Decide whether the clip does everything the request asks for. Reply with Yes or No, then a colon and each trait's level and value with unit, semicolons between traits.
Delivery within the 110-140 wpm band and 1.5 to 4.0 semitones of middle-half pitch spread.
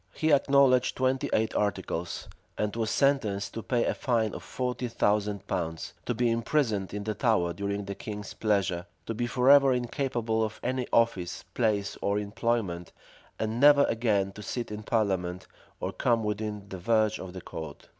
No: average, 170 wpm; average, 3.4 semitones